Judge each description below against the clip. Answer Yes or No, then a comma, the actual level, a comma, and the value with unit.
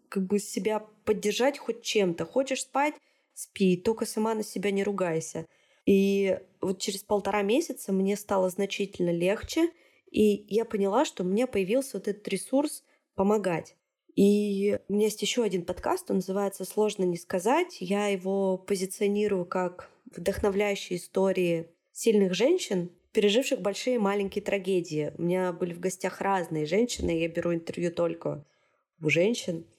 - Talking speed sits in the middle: Yes, average, 145 wpm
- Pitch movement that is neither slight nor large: Yes, average, 3.2 semitones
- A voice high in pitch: Yes, high, 200 Hz